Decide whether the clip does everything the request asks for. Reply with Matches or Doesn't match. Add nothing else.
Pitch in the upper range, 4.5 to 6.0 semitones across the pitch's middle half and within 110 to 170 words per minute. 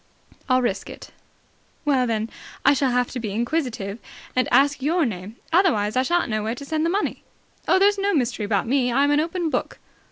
Doesn't match